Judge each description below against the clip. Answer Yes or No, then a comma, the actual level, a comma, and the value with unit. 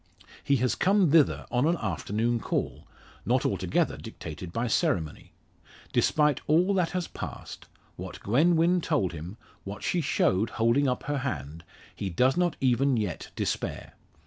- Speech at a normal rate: Yes, average, 150 wpm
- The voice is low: Yes, low, 125 Hz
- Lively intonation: Yes, wide, 7.9 semitones